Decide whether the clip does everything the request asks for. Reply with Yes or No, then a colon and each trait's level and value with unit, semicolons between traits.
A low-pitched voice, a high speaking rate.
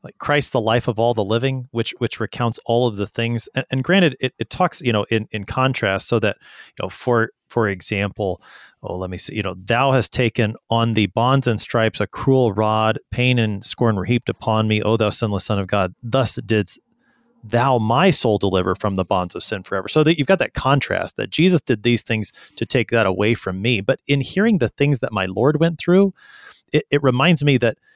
Yes: low, 120 Hz; fast, 230 wpm